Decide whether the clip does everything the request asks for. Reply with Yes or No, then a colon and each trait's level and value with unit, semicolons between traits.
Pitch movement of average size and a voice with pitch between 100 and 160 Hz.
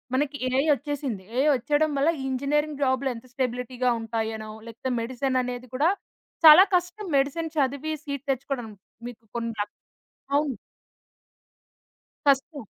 No: average, 3.0 semitones; very high, 265 Hz